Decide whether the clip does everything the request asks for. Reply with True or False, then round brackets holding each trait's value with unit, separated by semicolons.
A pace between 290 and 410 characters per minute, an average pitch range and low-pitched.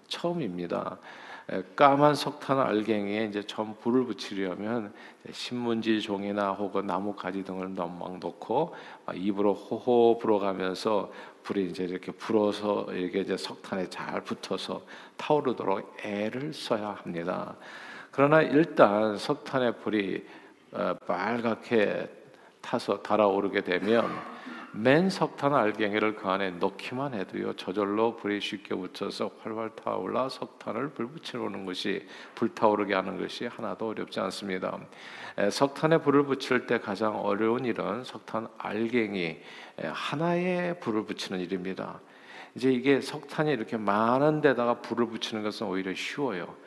True (295 characters per minute; 4.3 semitones; 110 Hz)